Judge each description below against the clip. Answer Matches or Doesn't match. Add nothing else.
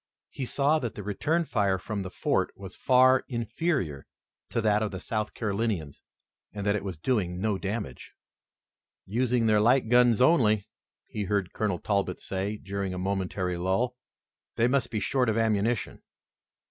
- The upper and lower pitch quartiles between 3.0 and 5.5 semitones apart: Matches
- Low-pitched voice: Matches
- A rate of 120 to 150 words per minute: Doesn't match